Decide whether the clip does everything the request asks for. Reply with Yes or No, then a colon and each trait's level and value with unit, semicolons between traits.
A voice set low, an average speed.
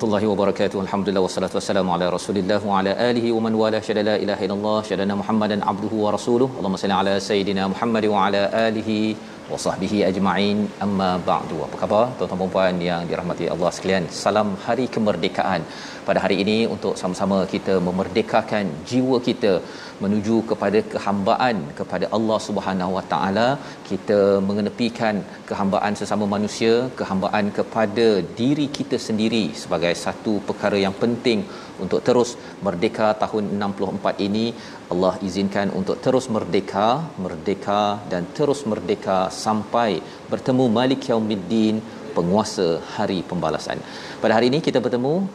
No: low, 105 Hz; fast, 140 wpm